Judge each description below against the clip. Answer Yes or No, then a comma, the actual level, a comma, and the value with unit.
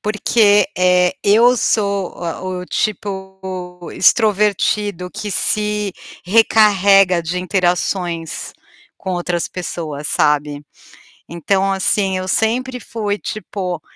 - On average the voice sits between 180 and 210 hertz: Yes, high, 190 Hz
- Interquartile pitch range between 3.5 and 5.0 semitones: No, average, 2.7 semitones